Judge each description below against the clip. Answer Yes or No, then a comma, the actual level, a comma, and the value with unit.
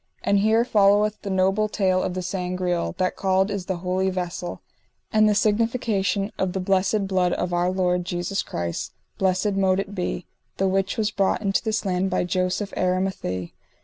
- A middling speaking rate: Yes, average, 180 wpm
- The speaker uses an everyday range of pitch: No, narrow, 1.8 semitones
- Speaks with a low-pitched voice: No, high, 190 Hz